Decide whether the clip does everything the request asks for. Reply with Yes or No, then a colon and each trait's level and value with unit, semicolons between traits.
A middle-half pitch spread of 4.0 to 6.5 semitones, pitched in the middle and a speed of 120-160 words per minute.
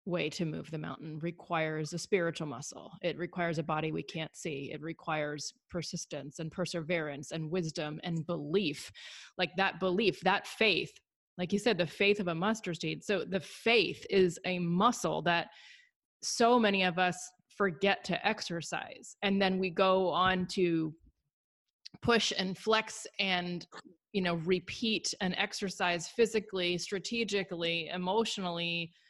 No: average, 2.9 semitones; medium, 180 Hz; average, 145 wpm